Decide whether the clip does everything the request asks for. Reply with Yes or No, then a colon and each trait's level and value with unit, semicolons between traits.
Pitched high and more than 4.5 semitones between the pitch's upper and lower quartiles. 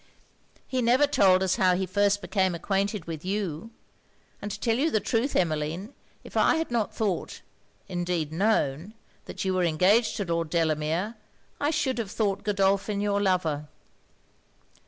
No: high, 195 Hz; average, 3.9 semitones